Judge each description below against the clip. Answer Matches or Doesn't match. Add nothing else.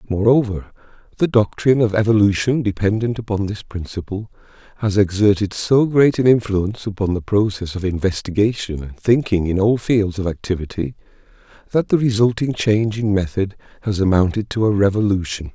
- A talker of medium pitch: Doesn't match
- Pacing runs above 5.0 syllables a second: Matches